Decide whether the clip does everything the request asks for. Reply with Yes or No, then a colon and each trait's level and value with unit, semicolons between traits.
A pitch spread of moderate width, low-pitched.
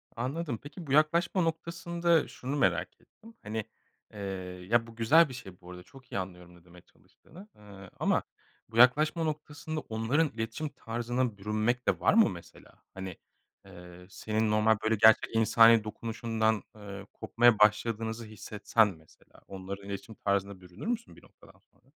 No: wide, 5.9 semitones; low, 115 Hz